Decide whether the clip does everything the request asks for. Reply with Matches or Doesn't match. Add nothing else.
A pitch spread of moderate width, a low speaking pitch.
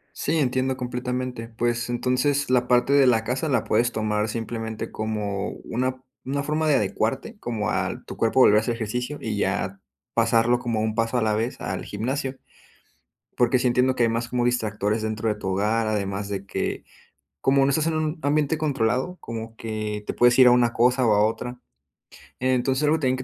Matches